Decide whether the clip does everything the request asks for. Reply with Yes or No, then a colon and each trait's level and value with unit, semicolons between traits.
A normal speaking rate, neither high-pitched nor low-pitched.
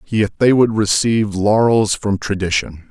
No: average, 145 wpm; low, 105 Hz